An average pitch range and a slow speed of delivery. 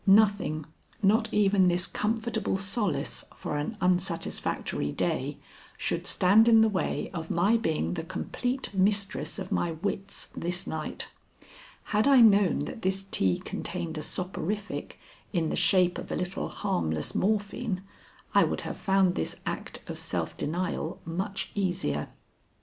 No: average, 3.4 semitones; average, 145 wpm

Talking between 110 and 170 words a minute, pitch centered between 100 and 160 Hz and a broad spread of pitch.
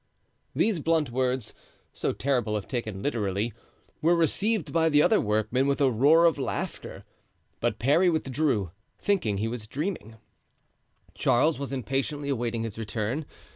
Yes: average, 140 wpm; low, 135 Hz; wide, 5.7 semitones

